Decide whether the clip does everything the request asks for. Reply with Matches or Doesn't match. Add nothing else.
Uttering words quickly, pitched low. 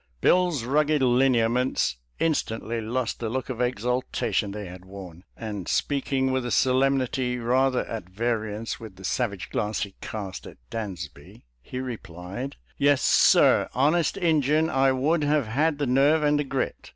Doesn't match